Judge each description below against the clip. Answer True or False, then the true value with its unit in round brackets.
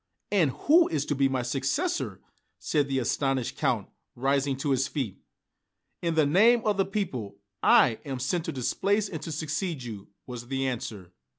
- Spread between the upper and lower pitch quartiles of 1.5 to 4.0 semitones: False (4.8 semitones)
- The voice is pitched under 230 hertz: True (140 Hz)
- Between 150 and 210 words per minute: True (175 wpm)